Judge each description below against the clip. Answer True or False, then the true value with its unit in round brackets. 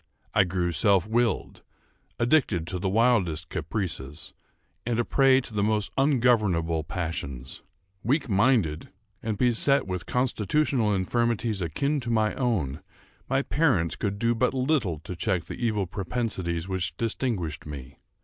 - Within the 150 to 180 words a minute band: False (140 wpm)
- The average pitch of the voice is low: True (105 Hz)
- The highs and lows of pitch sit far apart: True (6.0 semitones)